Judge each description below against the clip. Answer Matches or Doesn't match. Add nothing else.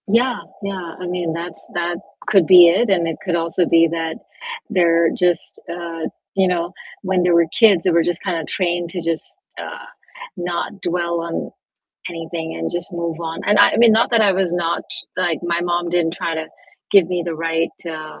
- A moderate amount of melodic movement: Doesn't match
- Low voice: Doesn't match